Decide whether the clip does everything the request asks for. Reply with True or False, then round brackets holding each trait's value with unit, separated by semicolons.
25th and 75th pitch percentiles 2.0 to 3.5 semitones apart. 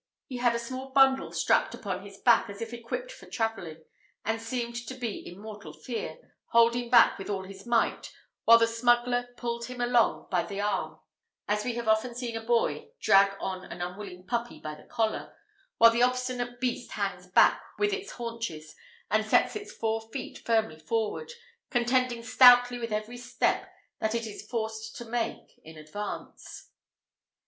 True (2.8 semitones)